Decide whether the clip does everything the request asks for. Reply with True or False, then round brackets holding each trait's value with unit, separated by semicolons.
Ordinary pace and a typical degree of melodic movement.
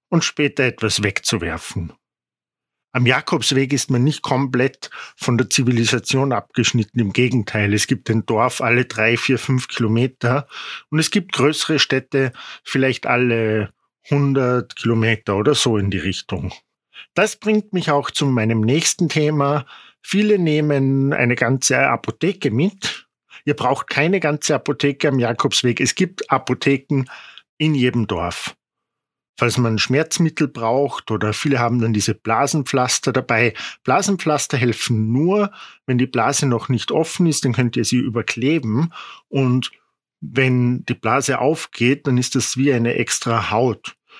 True (140 wpm; 3.7 semitones)